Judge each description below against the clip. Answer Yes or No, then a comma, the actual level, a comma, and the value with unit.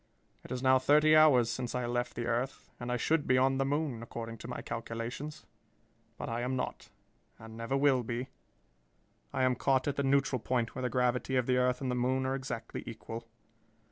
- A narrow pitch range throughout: Yes, narrow, 2.0 semitones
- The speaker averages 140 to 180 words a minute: No, fast, 205 wpm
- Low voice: Yes, low, 125 Hz